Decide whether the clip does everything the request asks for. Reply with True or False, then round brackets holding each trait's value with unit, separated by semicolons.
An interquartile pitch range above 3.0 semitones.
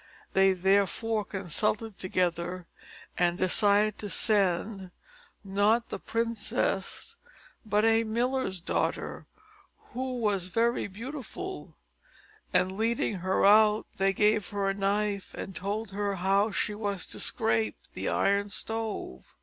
False (2.6 semitones)